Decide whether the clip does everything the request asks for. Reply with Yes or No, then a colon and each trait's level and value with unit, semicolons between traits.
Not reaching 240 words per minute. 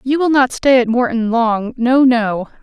Yes: fast, 205 wpm